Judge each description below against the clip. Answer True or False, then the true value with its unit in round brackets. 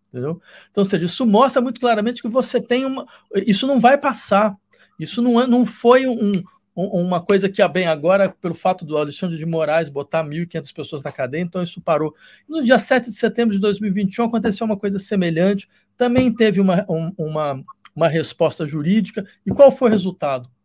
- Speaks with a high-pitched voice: True (195 Hz)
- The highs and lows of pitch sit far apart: True (6.2 semitones)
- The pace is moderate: False (195 wpm)